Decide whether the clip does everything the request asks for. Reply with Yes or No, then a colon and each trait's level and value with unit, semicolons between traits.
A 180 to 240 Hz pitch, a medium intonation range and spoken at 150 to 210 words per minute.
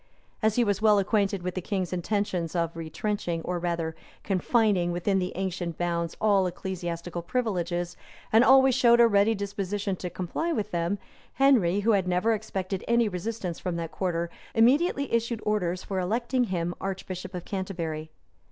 Yes: high, 190 Hz; average, 3.7 semitones; average, 160 wpm